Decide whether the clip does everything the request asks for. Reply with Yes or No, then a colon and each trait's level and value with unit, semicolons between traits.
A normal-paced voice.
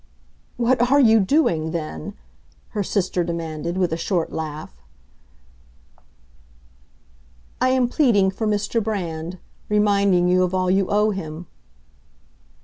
No: slow, 115 wpm